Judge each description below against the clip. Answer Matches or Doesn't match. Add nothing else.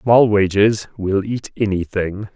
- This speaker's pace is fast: Doesn't match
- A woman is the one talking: Doesn't match